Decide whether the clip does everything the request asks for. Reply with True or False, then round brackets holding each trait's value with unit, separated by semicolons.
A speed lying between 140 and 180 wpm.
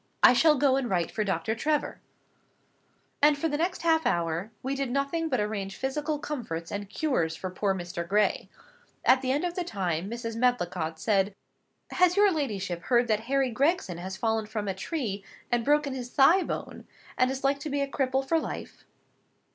False (190 wpm)